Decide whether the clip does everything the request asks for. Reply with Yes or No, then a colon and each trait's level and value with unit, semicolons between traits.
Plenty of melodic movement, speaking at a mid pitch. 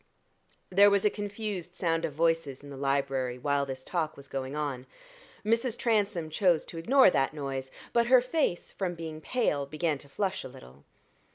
Yes: wide, 6.5 semitones; medium, 165 Hz